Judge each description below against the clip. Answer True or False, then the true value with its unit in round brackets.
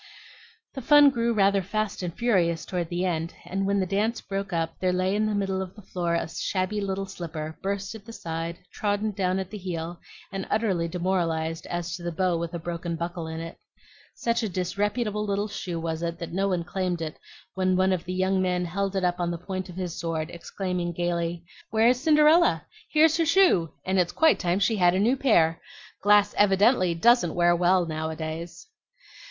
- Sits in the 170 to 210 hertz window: True (185 Hz)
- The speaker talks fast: True (210 wpm)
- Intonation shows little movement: False (3.0 semitones)